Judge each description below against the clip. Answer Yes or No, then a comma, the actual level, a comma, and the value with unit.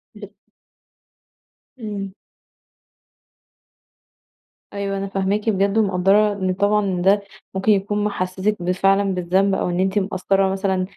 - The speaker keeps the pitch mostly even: Yes, narrow, 1.3 semitones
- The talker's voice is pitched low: No, high, 195 Hz